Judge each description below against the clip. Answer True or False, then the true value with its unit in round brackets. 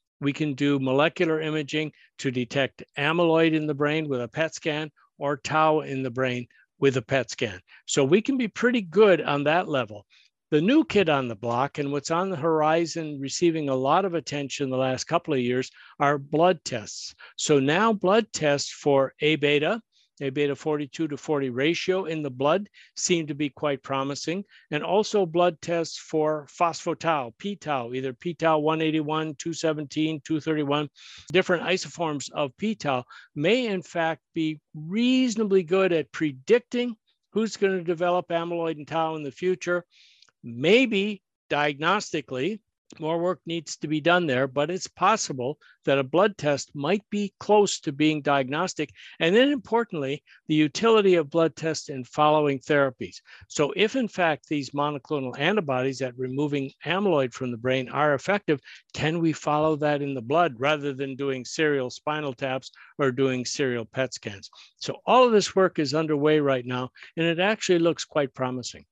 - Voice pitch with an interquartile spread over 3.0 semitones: True (4.0 semitones)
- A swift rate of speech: False (170 wpm)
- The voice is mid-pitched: True (155 Hz)